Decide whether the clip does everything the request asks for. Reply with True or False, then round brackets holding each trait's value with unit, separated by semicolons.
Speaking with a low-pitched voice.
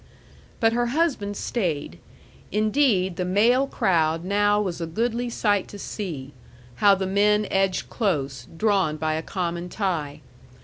False (195 Hz)